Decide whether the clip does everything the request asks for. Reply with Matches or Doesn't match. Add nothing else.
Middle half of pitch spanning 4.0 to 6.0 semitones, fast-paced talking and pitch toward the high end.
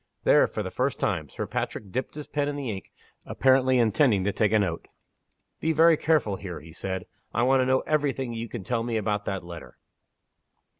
Doesn't match